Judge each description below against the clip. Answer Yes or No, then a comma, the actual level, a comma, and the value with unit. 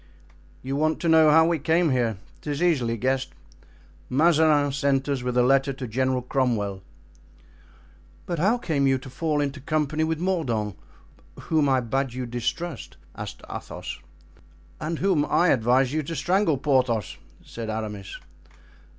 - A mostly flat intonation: No, average, 4.1 semitones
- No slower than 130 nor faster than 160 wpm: Yes, average, 150 wpm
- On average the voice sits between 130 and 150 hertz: Yes, medium, 140 Hz